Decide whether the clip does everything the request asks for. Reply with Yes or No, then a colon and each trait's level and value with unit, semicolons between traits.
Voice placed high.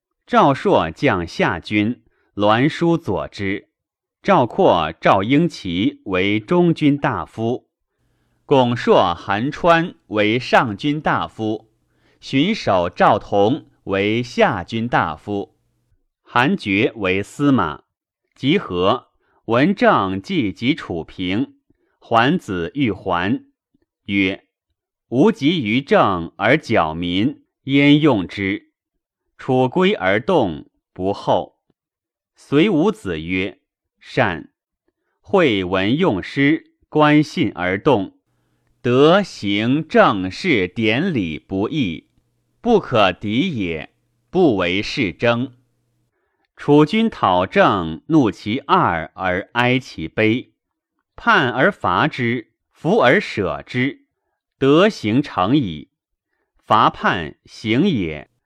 No: low, 120 Hz